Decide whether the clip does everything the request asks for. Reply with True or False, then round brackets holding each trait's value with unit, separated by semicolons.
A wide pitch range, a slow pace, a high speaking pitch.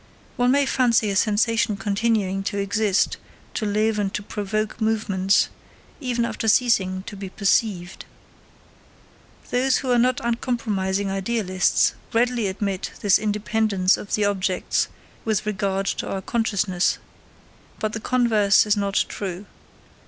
False (2.7 semitones; 130 wpm; 210 Hz)